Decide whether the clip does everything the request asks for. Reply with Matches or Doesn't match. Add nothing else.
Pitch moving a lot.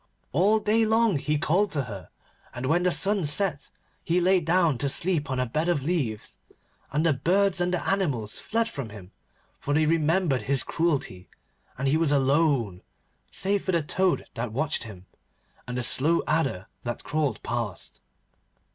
Matches